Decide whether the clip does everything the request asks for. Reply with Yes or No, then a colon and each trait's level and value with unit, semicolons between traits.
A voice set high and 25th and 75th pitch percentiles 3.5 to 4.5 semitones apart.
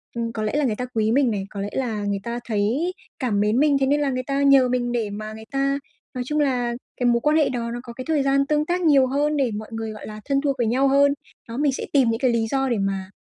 Yes: very high, 250 Hz; average, 3.8 semitones